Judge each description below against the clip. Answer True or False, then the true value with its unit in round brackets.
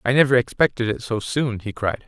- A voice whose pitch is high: False (120 Hz)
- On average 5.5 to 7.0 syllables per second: True (5.6 syllables/s)